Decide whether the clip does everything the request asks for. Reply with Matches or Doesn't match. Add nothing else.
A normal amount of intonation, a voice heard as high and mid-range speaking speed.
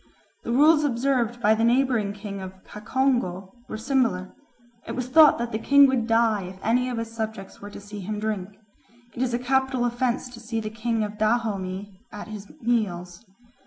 Matches